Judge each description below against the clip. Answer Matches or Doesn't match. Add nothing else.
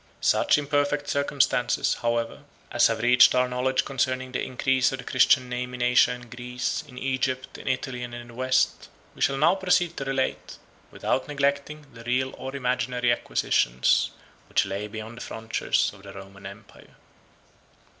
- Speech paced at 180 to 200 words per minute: Doesn't match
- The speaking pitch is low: Matches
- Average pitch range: Doesn't match